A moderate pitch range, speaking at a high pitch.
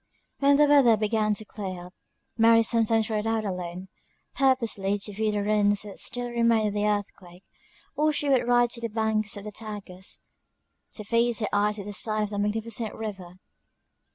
No: narrow, 2.1 semitones; high, 215 Hz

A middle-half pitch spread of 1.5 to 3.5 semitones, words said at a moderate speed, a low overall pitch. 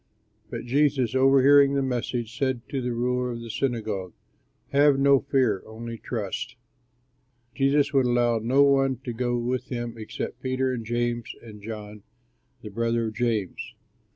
Yes: narrow, 2.6 semitones; average, 155 wpm; low, 120 Hz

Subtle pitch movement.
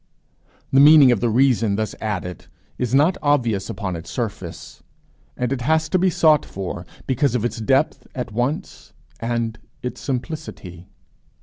No: average, 5.2 semitones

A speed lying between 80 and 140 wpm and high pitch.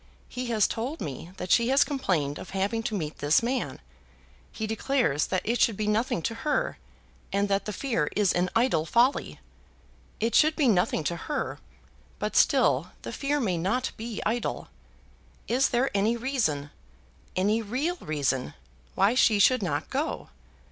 No: average, 165 wpm; high, 220 Hz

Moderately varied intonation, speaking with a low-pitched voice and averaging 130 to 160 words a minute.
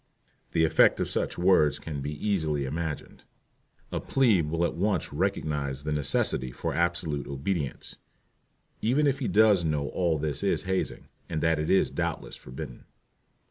Yes: average, 4.4 semitones; very low, 80 Hz; average, 155 wpm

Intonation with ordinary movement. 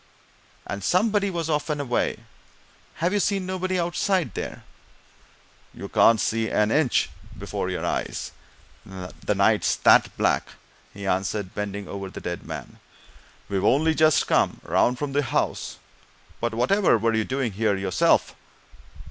No: wide, 8.8 semitones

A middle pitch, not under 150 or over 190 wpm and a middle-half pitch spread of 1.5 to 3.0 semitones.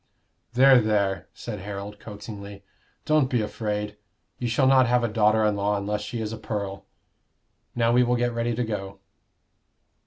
No: low, 110 Hz; average, 165 wpm; average, 2.7 semitones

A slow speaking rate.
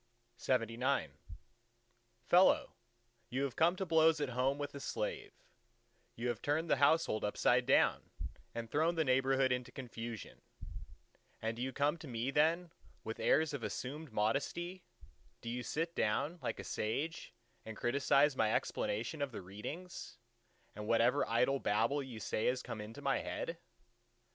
No: average, 150 wpm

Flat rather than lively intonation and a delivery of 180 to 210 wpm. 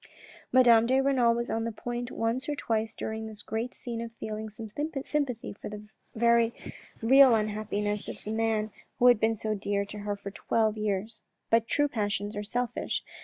Yes: narrow, 2.0 semitones; average, 185 wpm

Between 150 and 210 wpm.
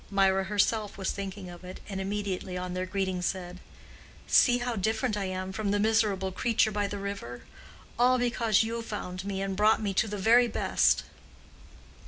Yes: average, 180 wpm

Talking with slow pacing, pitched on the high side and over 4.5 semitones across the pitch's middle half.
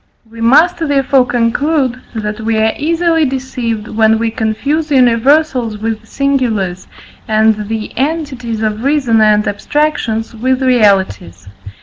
No: slow, 120 wpm; high, 230 Hz; average, 4.1 semitones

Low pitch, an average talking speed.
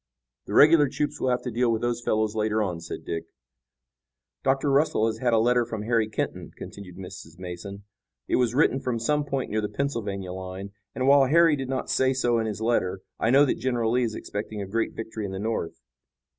No: low, 115 Hz; fast, 215 wpm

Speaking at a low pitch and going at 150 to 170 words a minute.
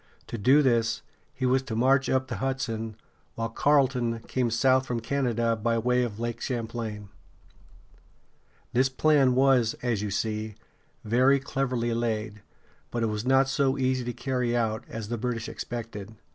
Yes: low, 120 Hz; average, 160 wpm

